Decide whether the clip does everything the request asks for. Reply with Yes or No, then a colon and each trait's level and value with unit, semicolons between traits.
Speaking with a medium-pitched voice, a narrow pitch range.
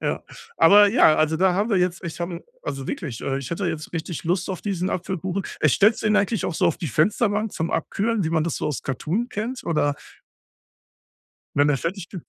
No: medium, 175 Hz; average, 4.2 semitones